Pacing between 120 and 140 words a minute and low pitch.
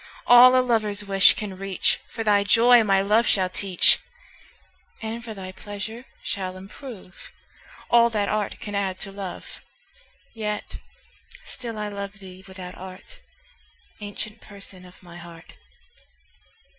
No: slow, 135 wpm; high, 200 Hz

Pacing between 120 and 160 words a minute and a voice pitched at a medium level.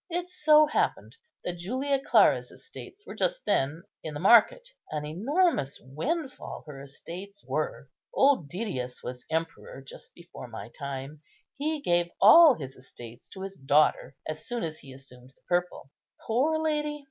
Yes: average, 155 wpm; medium, 175 Hz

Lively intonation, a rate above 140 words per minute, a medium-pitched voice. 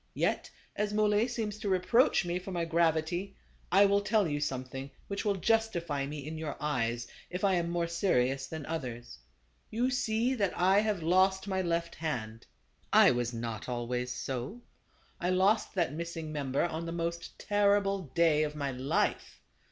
Yes: wide, 5.9 semitones; average, 170 wpm; medium, 170 Hz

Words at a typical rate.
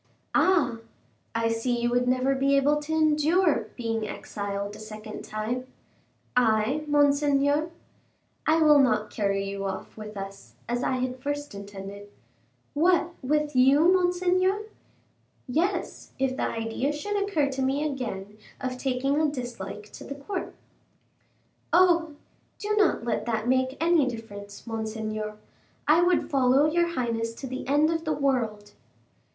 Yes: average, 145 wpm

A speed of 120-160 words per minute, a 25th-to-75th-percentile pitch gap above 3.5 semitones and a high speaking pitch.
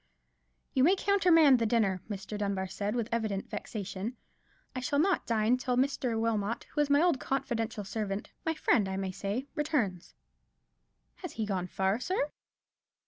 Yes: average, 150 wpm; wide, 5.5 semitones; high, 230 Hz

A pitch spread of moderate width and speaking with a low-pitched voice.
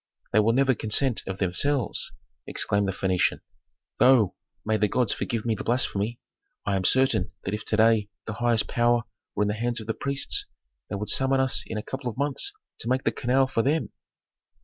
Yes: average, 3.8 semitones; low, 115 Hz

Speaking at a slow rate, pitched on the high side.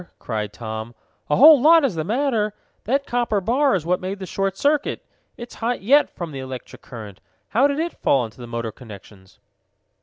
No: average, 190 wpm; high, 195 Hz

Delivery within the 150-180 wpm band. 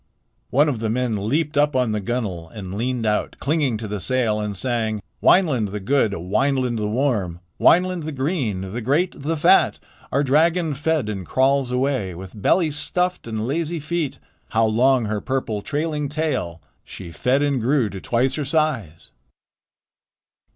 Yes: average, 165 wpm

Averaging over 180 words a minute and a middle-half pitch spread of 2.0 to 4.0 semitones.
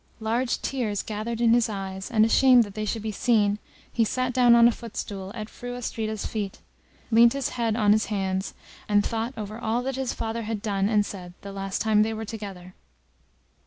Yes: average, 200 wpm; narrow, 2.4 semitones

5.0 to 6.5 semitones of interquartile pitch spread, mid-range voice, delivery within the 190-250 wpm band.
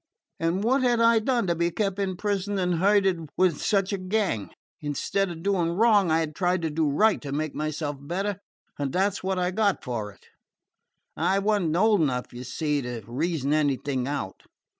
Yes: average, 5.3 semitones; medium, 175 Hz; average, 200 wpm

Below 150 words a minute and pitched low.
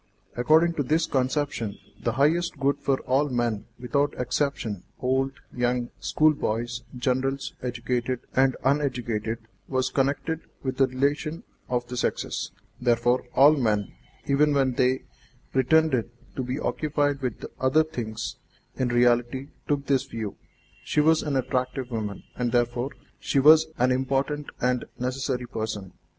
Yes: slow, 135 wpm; low, 130 Hz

